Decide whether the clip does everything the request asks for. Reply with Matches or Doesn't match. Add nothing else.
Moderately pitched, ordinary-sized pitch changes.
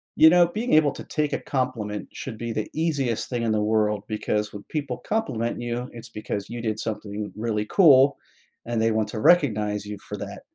Doesn't match